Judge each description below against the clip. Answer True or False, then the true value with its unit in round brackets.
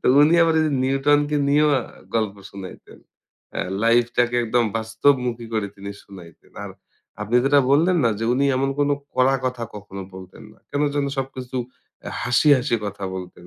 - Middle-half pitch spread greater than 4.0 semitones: True (4.6 semitones)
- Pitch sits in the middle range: False (125 Hz)